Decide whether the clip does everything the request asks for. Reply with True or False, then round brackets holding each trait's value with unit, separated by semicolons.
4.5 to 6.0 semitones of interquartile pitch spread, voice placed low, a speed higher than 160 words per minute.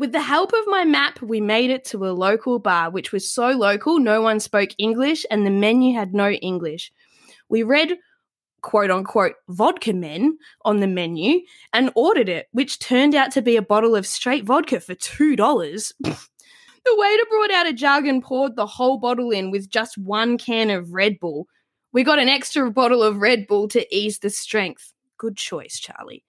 False (5.1 semitones; 235 Hz; 195 wpm)